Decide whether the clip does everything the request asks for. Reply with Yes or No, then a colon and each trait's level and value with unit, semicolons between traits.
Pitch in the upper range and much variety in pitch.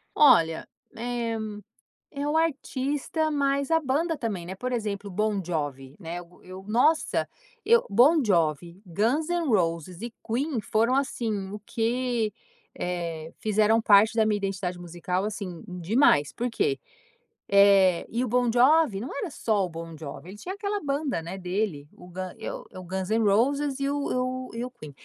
Yes: high, 215 Hz; wide, 6.4 semitones